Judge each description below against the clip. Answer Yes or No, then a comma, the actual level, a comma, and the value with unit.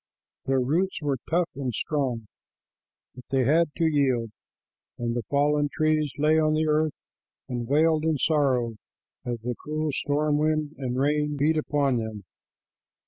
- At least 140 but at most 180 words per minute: Yes, average, 150 wpm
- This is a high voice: No, medium, 145 Hz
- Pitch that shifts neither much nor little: Yes, average, 3.2 semitones